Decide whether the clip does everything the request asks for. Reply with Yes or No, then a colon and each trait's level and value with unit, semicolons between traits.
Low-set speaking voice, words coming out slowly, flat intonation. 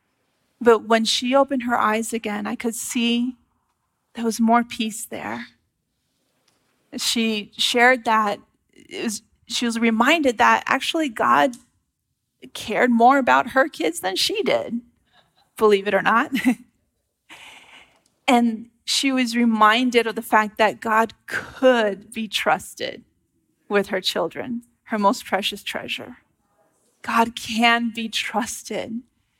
No: high, 235 Hz; slow, 125 wpm; narrow, 2.0 semitones